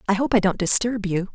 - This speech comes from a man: No, female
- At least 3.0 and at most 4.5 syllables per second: No, 6.1 syllables/s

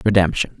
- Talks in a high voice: No, very low, 95 Hz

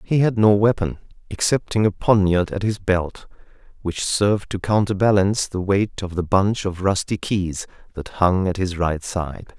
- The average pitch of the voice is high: No, low, 100 Hz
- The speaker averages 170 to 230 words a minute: Yes, average, 175 wpm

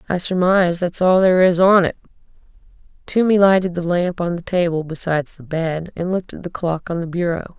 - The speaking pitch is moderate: Yes, medium, 175 Hz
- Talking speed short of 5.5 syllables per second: No, 5.7 syllables/s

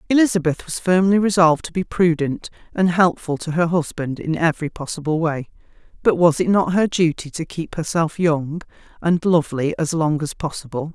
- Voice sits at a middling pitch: Yes, medium, 165 Hz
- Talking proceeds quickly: No, average, 175 wpm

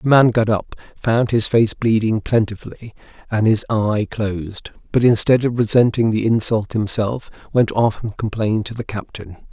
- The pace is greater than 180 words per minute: No, average, 170 wpm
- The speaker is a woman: No, male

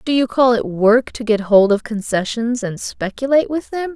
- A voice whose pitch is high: Yes, high, 235 Hz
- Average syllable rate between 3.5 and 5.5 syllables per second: Yes, 4.9 syllables/s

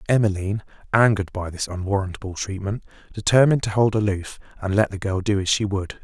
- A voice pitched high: No, low, 100 Hz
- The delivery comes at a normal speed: Yes, average, 180 wpm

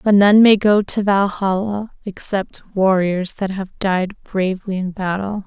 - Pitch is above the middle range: Yes, high, 195 Hz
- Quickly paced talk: No, average, 155 wpm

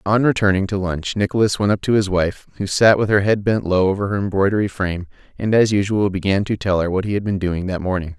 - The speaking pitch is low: Yes, low, 100 Hz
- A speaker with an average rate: No, fast, 255 wpm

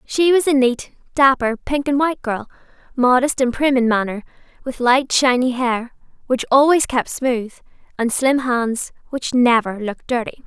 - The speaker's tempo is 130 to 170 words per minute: Yes, average, 165 wpm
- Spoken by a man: No, female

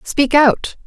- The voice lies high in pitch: Yes, very high, 275 Hz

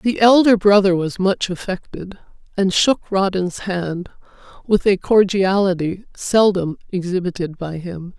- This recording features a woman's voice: Yes, female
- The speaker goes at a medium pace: No, slow, 125 wpm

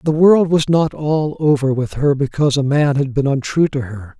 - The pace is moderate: No, fast, 230 wpm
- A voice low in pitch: No, medium, 145 Hz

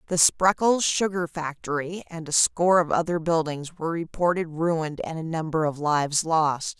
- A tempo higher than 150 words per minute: Yes, average, 170 wpm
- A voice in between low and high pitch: Yes, medium, 165 Hz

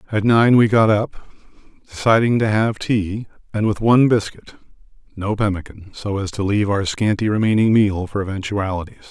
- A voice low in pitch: Yes, low, 105 Hz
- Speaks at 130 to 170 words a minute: Yes, average, 165 wpm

